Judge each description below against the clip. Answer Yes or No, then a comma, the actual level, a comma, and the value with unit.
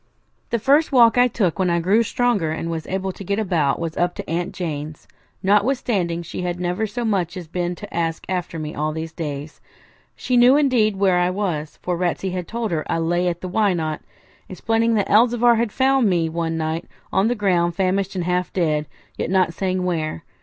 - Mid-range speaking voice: Yes, medium, 180 Hz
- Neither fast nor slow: No, fast, 210 wpm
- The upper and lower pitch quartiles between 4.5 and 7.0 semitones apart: No, average, 4.1 semitones